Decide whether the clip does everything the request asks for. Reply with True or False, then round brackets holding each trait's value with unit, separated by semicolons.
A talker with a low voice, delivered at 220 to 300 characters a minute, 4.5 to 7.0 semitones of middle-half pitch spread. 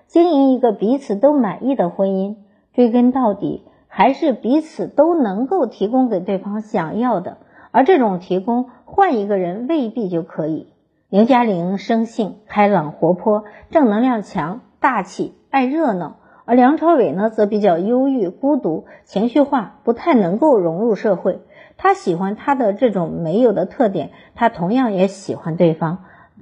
False (220 Hz; 240 characters per minute; 5.1 semitones)